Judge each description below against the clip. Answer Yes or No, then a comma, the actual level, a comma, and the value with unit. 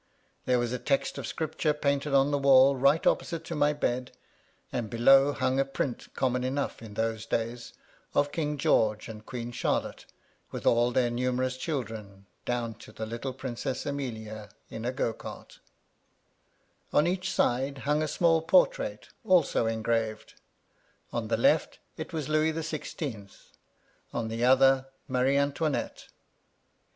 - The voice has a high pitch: No, low, 130 Hz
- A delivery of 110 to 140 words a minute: No, average, 150 wpm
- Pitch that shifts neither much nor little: Yes, average, 3.6 semitones